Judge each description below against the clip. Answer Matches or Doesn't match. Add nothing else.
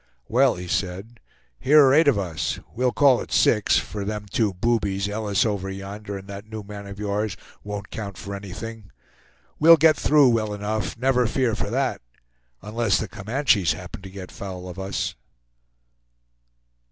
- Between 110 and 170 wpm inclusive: Matches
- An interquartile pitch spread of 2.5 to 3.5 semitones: Matches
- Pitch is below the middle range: Matches